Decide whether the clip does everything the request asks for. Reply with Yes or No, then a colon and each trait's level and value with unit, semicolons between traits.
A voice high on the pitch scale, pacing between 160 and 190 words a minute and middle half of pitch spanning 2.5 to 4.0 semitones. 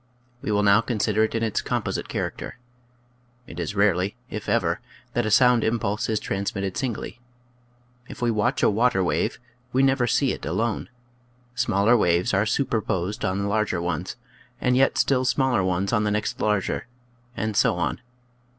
No: low, 105 Hz; average, 170 wpm; average, 3.4 semitones